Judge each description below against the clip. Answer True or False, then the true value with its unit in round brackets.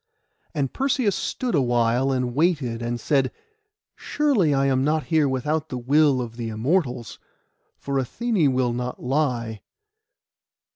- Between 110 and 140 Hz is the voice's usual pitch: True (135 Hz)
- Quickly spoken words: False (145 wpm)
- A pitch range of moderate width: True (4.1 semitones)